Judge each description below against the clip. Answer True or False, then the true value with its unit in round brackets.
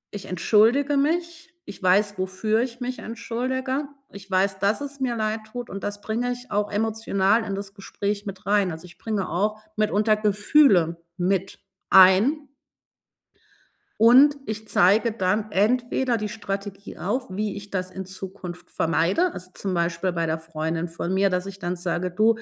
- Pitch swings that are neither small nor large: True (3.7 semitones)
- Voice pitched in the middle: False (205 Hz)